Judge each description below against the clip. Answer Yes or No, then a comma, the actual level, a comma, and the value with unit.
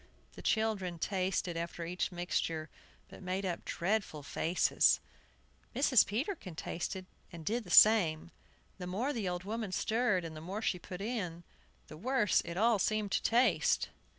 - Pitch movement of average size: Yes, average, 4.2 semitones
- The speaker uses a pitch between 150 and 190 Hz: Yes, medium, 185 Hz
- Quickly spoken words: No, average, 155 wpm